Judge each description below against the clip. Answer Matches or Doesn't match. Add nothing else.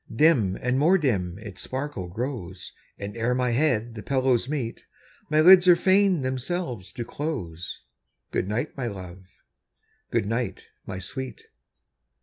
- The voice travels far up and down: Matches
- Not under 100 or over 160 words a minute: Matches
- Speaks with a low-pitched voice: Matches